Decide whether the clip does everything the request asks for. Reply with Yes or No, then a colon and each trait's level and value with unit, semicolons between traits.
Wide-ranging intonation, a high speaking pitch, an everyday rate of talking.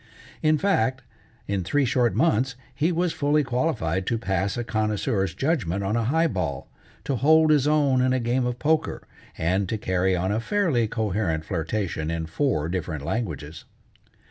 No: wide, 7.2 semitones; low, 115 Hz; average, 170 wpm